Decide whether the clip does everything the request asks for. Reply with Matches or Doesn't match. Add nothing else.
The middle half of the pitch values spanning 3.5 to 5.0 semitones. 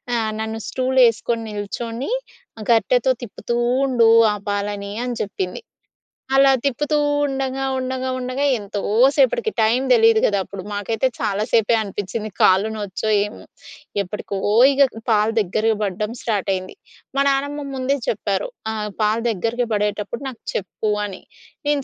Matches